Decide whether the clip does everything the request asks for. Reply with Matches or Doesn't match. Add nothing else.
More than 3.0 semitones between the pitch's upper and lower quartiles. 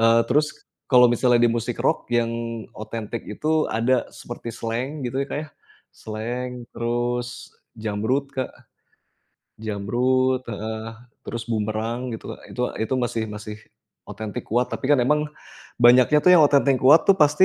Doesn't match